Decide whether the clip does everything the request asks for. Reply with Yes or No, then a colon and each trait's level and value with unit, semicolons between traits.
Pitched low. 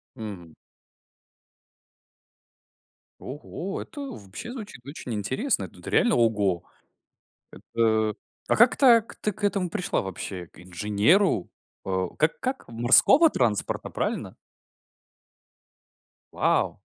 Yes: low, 120 Hz